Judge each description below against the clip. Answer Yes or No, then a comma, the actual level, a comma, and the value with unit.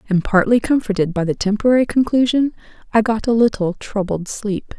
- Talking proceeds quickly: No, average, 165 wpm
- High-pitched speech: Yes, high, 215 Hz